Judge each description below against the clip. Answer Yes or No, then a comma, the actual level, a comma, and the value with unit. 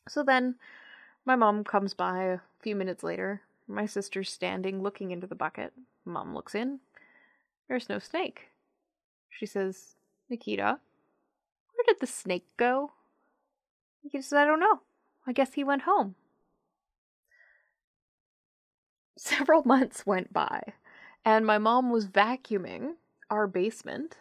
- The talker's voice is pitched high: Yes, high, 235 Hz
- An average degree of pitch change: No, wide, 6.1 semitones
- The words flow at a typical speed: No, slow, 130 wpm